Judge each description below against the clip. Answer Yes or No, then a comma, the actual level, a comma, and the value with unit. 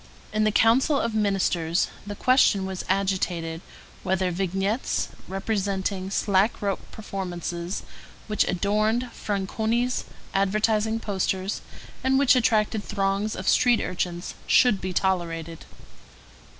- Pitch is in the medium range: No, high, 195 Hz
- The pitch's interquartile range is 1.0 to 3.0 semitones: Yes, narrow, 2.6 semitones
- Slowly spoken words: Yes, slow, 110 wpm